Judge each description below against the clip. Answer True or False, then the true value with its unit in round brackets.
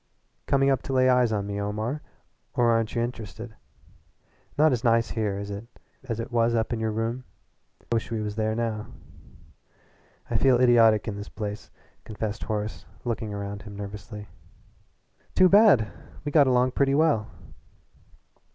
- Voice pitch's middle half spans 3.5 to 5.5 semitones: False (2.9 semitones)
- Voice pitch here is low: True (115 Hz)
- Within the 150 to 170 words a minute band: True (160 wpm)